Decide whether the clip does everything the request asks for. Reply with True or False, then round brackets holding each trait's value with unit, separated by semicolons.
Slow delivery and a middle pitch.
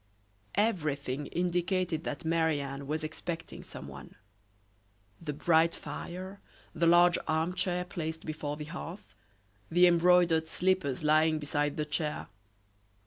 True (120 wpm; 160 Hz)